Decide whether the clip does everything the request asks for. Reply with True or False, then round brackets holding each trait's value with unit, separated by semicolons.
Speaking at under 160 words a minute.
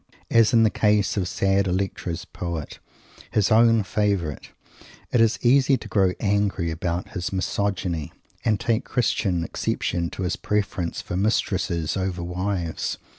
True (140 wpm)